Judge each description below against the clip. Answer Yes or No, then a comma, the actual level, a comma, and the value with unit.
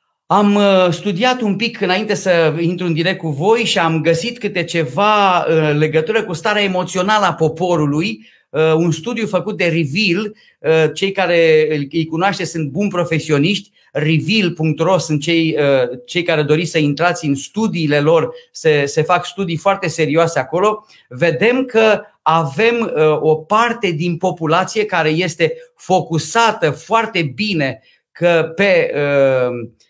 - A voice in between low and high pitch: Yes, medium, 175 Hz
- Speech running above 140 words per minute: No, average, 135 wpm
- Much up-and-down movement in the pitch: No, average, 4.3 semitones